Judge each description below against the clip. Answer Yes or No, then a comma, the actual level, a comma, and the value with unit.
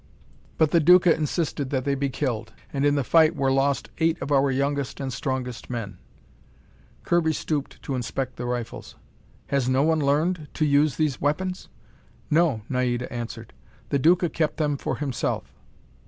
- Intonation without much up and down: No, average, 3.3 semitones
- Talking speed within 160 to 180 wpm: Yes, average, 165 wpm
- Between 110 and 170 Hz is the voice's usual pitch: Yes, medium, 140 Hz